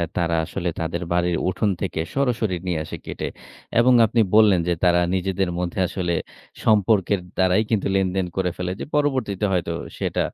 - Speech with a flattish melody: No, average, 3.4 semitones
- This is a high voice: No, very low, 95 Hz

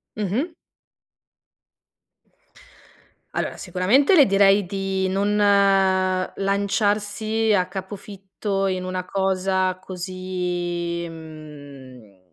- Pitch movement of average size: No, narrow, 1.7 semitones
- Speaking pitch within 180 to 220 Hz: Yes, high, 190 Hz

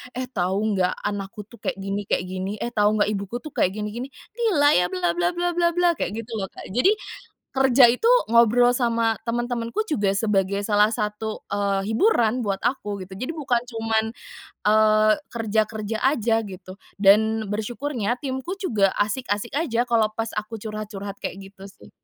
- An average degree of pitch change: Yes, average, 3.2 semitones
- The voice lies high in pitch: Yes, high, 220 Hz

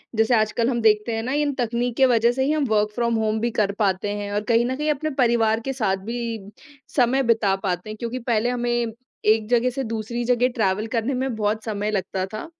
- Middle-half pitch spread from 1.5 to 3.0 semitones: Yes, narrow, 2.4 semitones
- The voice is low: No, high, 230 Hz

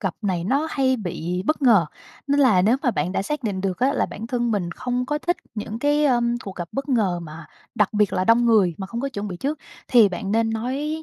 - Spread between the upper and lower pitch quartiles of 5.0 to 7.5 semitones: Yes, wide, 5.6 semitones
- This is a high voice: Yes, high, 225 Hz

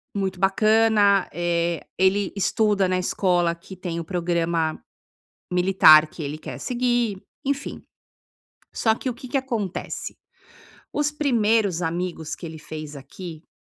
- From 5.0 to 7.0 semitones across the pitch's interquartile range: No, average, 4.5 semitones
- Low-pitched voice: No, medium, 185 Hz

